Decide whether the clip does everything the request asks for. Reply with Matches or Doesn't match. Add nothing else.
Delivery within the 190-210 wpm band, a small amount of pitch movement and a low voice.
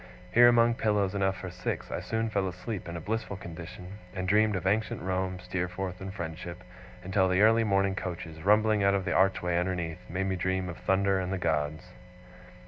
Matches